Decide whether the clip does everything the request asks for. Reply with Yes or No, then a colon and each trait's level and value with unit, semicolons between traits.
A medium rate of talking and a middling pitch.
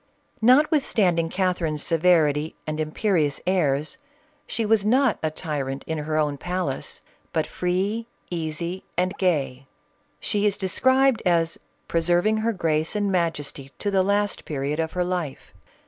Yes: average, 145 wpm; medium, 175 Hz